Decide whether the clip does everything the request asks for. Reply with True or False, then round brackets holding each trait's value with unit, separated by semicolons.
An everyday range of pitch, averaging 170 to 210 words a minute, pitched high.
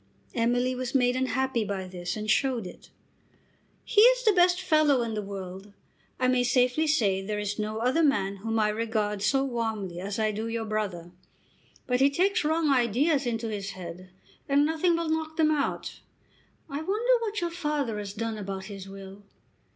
False (6.3 semitones; 180 wpm; 235 Hz)